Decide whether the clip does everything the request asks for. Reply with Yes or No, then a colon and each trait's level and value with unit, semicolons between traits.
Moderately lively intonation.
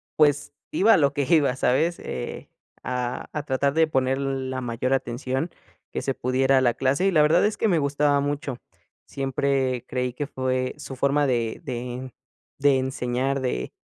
No: narrow, 2.1 semitones